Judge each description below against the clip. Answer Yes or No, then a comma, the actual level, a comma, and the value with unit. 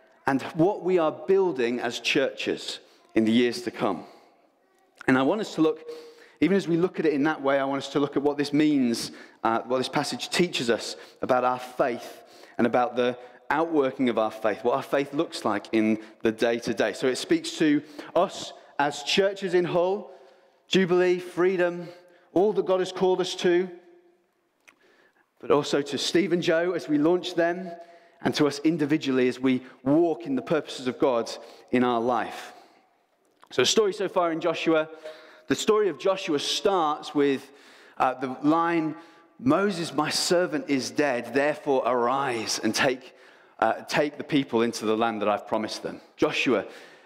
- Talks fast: No, average, 180 wpm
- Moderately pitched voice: Yes, medium, 160 Hz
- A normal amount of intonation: No, wide, 5.8 semitones